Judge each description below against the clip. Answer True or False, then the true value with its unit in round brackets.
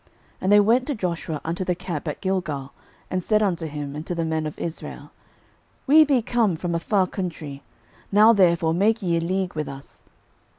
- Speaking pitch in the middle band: True (175 Hz)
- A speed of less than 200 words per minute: False (205 wpm)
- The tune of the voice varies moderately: True (4.3 semitones)